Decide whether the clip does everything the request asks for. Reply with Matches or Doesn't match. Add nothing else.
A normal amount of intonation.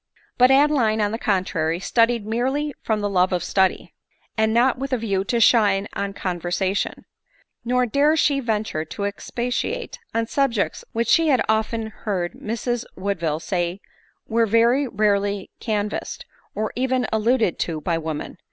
Matches